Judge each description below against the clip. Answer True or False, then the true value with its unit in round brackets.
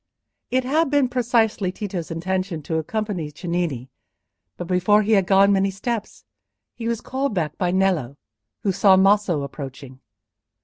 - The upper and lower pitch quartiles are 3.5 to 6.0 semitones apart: True (4.5 semitones)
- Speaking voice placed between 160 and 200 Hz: True (190 Hz)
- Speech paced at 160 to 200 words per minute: False (145 wpm)